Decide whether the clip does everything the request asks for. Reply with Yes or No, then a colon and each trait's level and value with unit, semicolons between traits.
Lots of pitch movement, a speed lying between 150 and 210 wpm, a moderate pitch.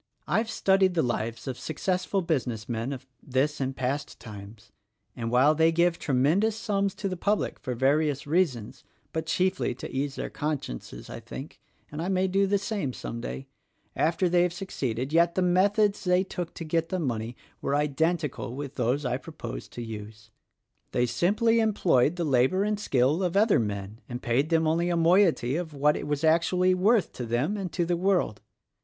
Yes: wide, 6.4 semitones; average, 190 wpm; medium, 155 Hz